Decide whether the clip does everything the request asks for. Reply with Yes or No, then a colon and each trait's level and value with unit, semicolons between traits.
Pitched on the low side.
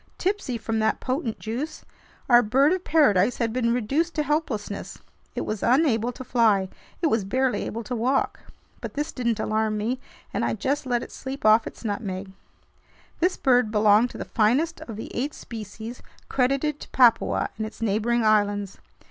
No: high, 235 Hz